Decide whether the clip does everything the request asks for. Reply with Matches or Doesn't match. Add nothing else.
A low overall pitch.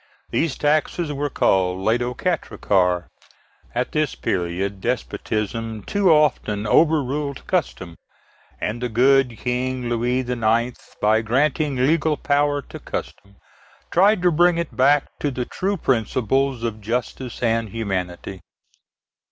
Matches